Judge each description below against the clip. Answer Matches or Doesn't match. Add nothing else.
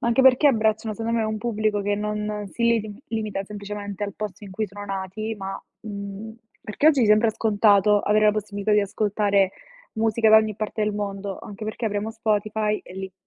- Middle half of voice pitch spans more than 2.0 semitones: Doesn't match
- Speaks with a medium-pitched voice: Doesn't match